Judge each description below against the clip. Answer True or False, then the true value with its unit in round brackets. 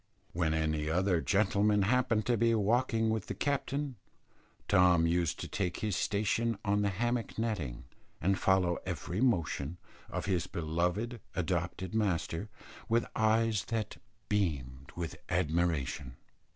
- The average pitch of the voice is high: False (95 Hz)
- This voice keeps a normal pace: False (130 wpm)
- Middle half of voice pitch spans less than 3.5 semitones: False (4.7 semitones)